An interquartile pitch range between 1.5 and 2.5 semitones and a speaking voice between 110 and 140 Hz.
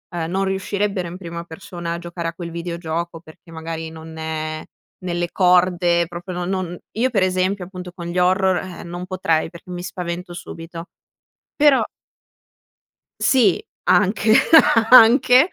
No: narrow, 2.0 semitones; medium, 175 Hz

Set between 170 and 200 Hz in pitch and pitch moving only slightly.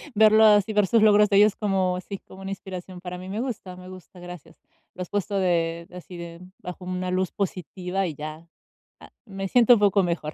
Yes: medium, 185 Hz; narrow, 2.3 semitones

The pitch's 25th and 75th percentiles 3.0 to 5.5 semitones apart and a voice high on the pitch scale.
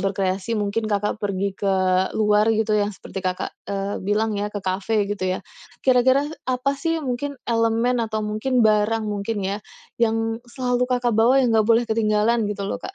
No: narrow, 2.6 semitones; high, 220 Hz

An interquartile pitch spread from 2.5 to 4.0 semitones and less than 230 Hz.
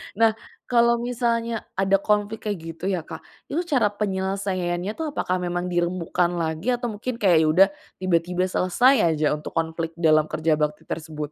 No: average, 4.9 semitones; medium, 185 Hz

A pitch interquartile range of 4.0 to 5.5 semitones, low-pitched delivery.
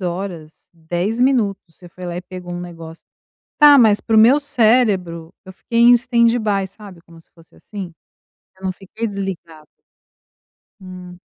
No: average, 4.3 semitones; high, 190 Hz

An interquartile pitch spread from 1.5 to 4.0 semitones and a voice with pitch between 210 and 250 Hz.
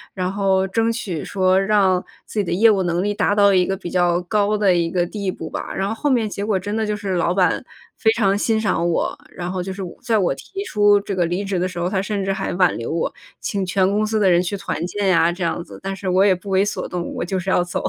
No: narrow, 2.4 semitones; high, 190 Hz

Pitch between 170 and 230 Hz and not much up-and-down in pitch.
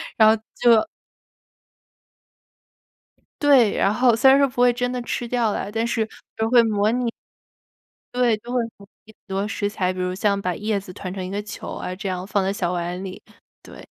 No: high, 215 Hz; average, 3.8 semitones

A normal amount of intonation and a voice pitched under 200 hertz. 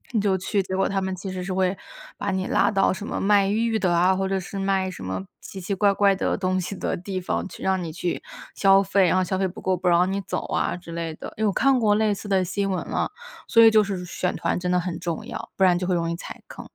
No: narrow, 1.7 semitones; high, 190 Hz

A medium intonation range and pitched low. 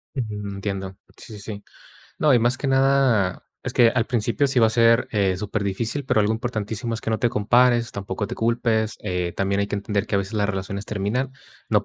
Yes: average, 3.1 semitones; low, 110 Hz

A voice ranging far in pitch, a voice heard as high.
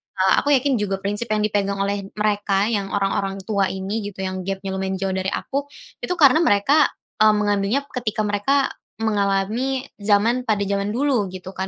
No: average, 2.7 semitones; high, 205 Hz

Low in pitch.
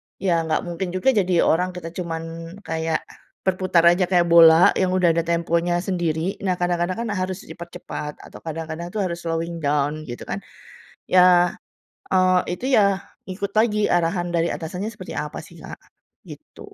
No: medium, 175 Hz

